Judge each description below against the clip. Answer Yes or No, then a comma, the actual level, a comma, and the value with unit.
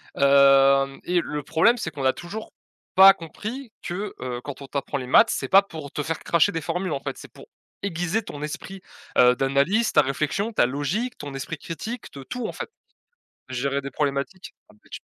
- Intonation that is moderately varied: No, wide, 5.9 semitones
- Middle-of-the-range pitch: Yes, medium, 150 Hz